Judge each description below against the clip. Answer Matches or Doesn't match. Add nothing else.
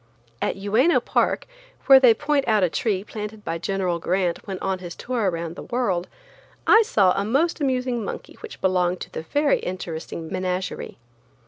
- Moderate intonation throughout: Doesn't match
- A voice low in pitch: Doesn't match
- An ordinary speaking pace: Matches